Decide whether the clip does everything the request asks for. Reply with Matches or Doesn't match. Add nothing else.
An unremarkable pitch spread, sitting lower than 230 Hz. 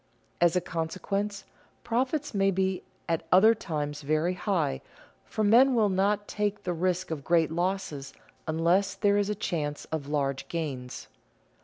Matches